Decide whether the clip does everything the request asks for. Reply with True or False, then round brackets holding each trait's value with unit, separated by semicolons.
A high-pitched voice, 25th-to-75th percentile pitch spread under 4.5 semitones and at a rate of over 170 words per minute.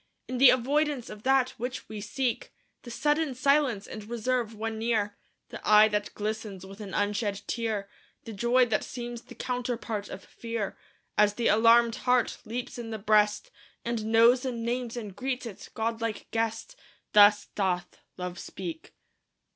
False (230 Hz; 2.9 semitones; 160 wpm)